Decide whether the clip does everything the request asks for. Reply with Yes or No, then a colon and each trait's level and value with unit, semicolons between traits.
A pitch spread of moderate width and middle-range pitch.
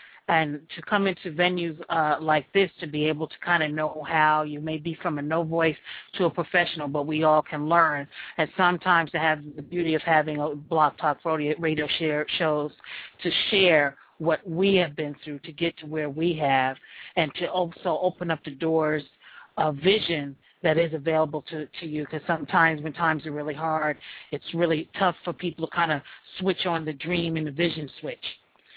No: narrow, 2.0 semitones; medium, 160 Hz